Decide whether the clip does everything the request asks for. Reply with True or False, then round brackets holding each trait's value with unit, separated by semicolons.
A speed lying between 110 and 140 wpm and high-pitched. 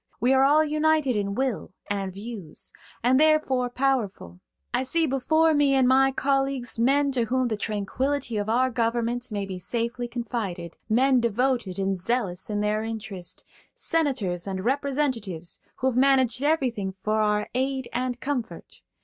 False (150 wpm; 245 Hz)